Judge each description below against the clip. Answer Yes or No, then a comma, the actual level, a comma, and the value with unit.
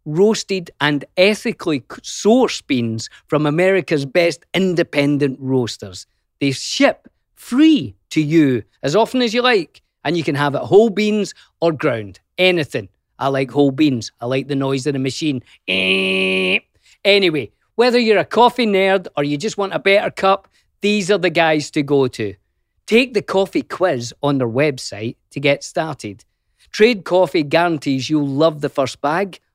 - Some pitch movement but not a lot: No, wide, 6.4 semitones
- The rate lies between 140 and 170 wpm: Yes, average, 160 wpm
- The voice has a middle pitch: Yes, medium, 155 Hz